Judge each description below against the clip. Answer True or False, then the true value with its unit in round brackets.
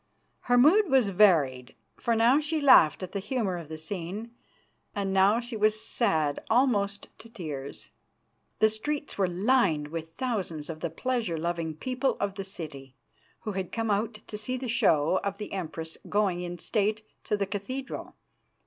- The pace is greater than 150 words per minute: True (170 wpm)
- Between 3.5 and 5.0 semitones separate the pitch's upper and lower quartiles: False (5.6 semitones)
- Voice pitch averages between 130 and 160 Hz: False (200 Hz)